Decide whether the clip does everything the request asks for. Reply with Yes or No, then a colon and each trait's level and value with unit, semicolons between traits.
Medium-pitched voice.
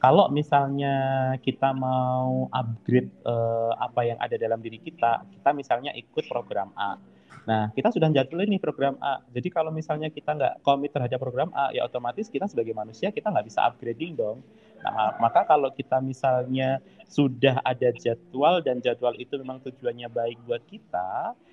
No: low, 130 Hz